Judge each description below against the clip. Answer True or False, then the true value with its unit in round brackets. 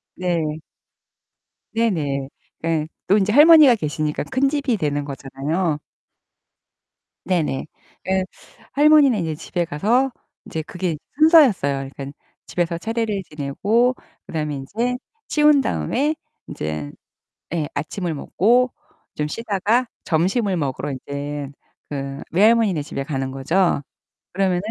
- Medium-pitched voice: True (175 Hz)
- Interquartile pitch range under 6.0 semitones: False (7.8 semitones)